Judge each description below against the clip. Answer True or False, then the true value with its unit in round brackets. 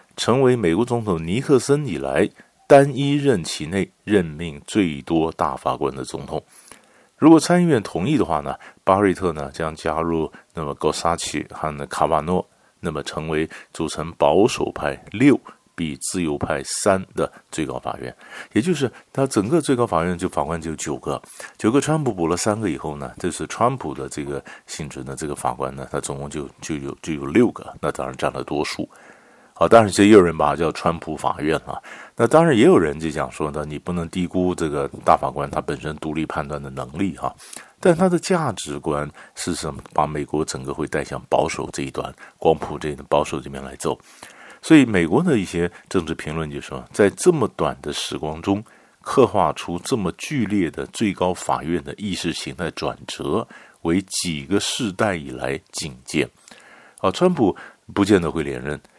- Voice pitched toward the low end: True (85 Hz)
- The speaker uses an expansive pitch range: True (5.9 semitones)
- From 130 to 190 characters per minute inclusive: False (275 characters per minute)